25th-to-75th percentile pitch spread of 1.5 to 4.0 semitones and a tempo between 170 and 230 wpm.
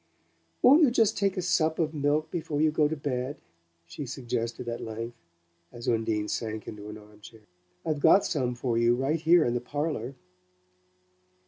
No: average, 5.2 semitones; average, 175 wpm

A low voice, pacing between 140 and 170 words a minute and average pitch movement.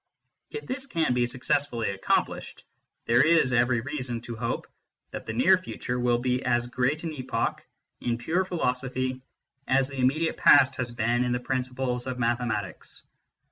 No: low, 125 Hz; average, 160 wpm; narrow, 2.1 semitones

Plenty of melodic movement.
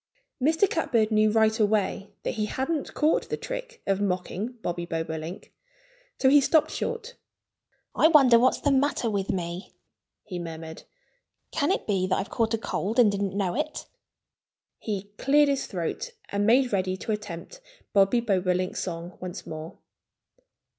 Yes: wide, 6.4 semitones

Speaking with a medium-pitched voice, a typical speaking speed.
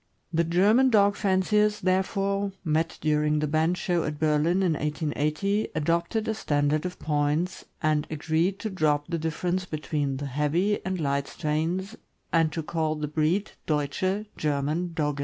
Yes: medium, 160 Hz; average, 160 wpm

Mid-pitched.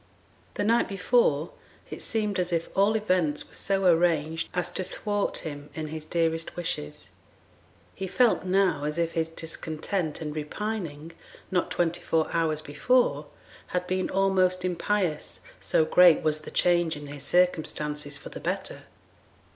Yes: medium, 170 Hz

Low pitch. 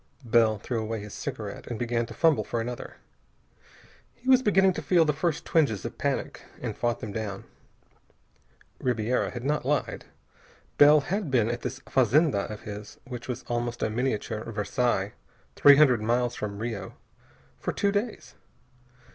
Yes: low, 120 Hz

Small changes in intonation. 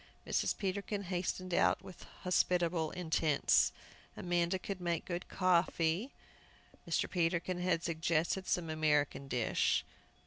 Yes: narrow, 2.1 semitones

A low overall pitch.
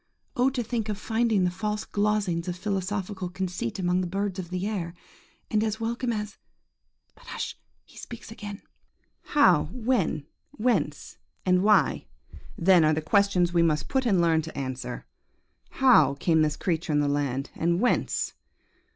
No: high, 190 Hz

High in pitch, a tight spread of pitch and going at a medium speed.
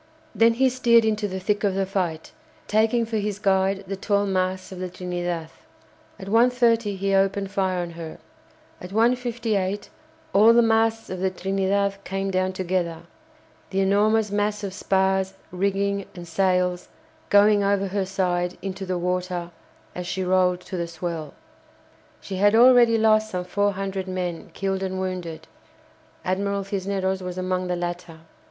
Yes: high, 195 Hz; narrow, 2.0 semitones; average, 160 wpm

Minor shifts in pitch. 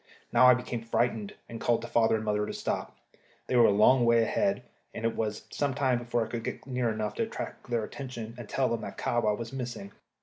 Yes: narrow, 2.1 semitones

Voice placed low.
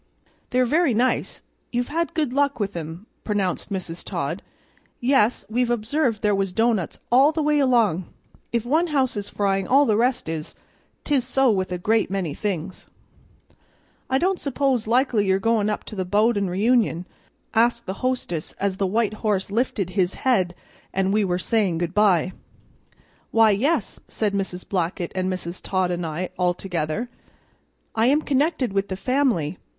No: high, 210 Hz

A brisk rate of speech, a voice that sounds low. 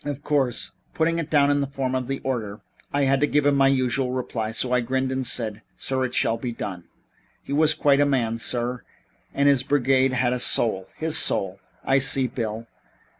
Yes: fast, 210 wpm; low, 130 Hz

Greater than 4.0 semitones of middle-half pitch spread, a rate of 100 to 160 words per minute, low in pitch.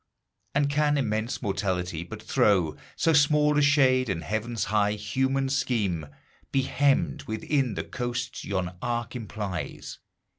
Yes: average, 5.3 semitones; slow, 135 wpm; low, 120 Hz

